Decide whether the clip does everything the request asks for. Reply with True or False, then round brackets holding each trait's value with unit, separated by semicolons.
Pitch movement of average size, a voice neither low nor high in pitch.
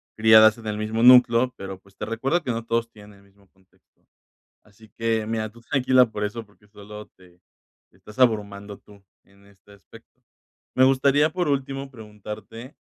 False (3.3 semitones; 110 Hz)